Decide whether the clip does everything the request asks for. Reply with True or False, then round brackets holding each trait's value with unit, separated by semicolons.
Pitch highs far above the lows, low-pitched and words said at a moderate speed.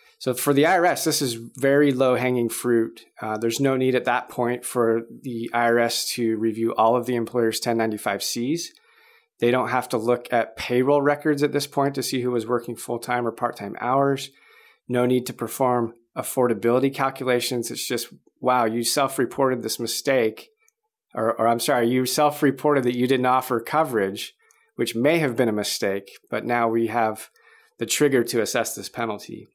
False (3.0 semitones; 125 Hz; 185 wpm)